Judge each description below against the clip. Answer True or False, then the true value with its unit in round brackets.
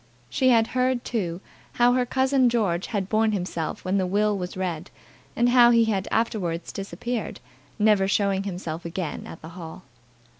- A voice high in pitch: True (200 Hz)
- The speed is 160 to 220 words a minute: True (165 wpm)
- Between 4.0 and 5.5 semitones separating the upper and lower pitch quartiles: True (4.8 semitones)